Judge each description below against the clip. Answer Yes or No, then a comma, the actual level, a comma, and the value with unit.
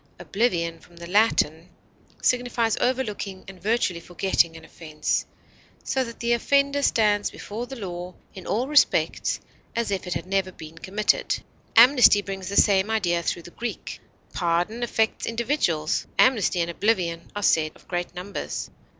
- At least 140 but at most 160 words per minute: Yes, average, 150 wpm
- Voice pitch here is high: Yes, high, 200 Hz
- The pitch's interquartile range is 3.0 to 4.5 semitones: No, average, 5.1 semitones